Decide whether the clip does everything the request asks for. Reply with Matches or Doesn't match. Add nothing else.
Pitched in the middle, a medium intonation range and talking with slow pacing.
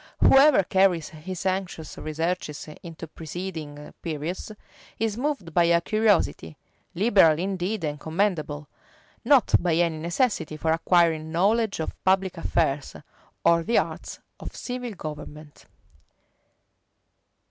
Matches